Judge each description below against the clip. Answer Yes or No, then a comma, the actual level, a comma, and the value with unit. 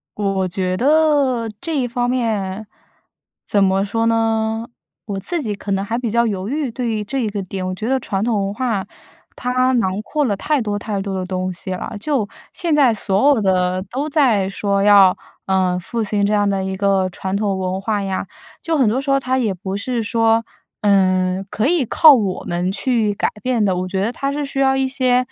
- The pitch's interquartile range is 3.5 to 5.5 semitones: Yes, average, 4.6 semitones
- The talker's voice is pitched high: Yes, high, 210 Hz